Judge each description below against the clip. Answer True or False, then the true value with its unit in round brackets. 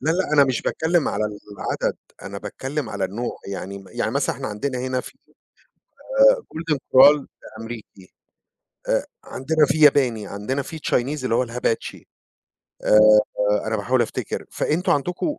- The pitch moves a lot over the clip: True (5.8 semitones)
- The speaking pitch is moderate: False (130 Hz)